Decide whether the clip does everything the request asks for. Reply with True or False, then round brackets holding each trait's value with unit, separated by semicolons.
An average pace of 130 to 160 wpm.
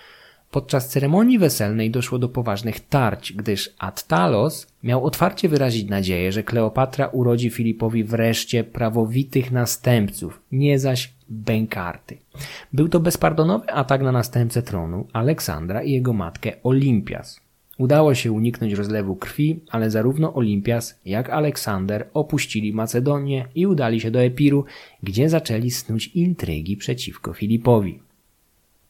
False (120 wpm)